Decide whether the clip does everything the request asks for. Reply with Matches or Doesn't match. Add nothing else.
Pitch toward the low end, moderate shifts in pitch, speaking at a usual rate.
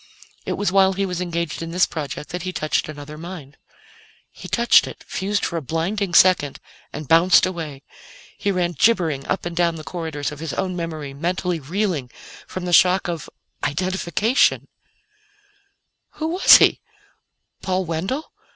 Doesn't match